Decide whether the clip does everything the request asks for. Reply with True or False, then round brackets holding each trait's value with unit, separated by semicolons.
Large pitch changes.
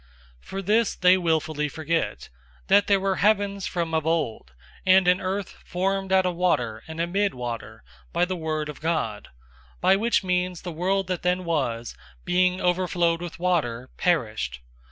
False (3.2 semitones)